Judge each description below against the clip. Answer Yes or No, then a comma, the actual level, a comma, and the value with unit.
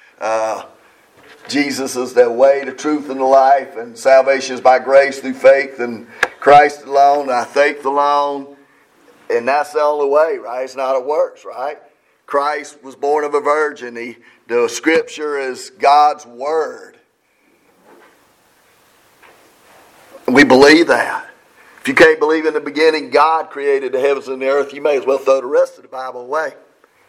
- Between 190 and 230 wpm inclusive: No, average, 165 wpm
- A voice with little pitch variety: Yes, narrow, 2.1 semitones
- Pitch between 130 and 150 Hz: Yes, medium, 140 Hz